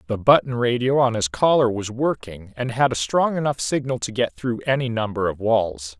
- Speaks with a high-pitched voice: No, low, 115 Hz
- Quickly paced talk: Yes, fast, 210 wpm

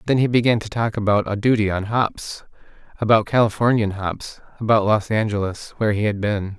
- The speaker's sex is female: No, male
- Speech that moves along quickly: No, average, 180 wpm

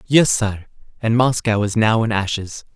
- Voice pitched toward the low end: Yes, low, 110 Hz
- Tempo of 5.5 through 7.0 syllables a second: No, 4.5 syllables/s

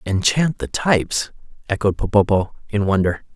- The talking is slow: Yes, slow, 125 wpm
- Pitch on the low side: Yes, low, 105 Hz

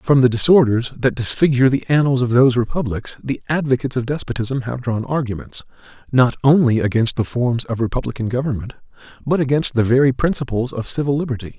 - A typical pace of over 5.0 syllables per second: Yes, 6.1 syllables/s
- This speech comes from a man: Yes, male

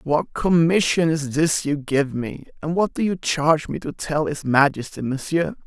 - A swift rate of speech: No, average, 190 wpm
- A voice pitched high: No, medium, 150 Hz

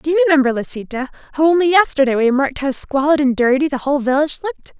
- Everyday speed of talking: No, fast, 215 wpm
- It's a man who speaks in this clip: No, female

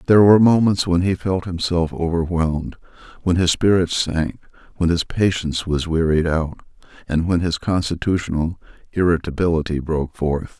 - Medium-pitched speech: No, very low, 85 Hz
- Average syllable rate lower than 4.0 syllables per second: No, 5.3 syllables/s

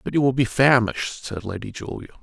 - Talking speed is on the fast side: Yes, fast, 215 wpm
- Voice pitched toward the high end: No, low, 120 Hz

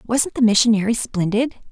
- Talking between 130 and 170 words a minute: Yes, average, 140 wpm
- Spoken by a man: No, female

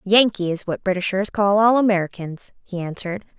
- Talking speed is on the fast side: No, average, 160 wpm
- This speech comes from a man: No, female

